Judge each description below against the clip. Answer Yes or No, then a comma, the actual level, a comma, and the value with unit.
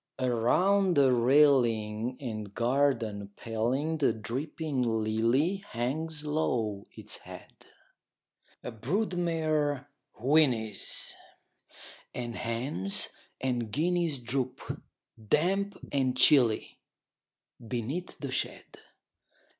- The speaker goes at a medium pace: No, slow, 85 wpm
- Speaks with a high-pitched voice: No, low, 130 Hz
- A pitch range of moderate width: Yes, average, 4.9 semitones